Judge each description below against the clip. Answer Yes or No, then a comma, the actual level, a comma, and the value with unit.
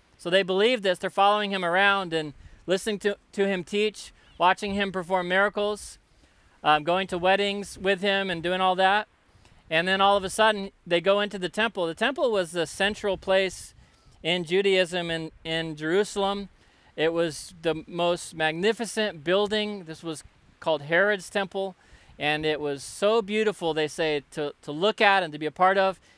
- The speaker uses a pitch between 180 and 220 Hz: Yes, medium, 185 Hz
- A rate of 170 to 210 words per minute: Yes, average, 180 wpm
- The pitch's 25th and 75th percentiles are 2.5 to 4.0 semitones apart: Yes, average, 3.6 semitones